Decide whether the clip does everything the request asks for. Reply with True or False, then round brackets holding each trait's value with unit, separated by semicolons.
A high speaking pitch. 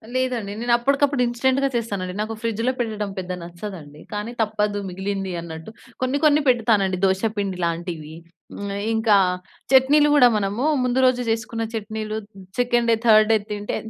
True (215 Hz)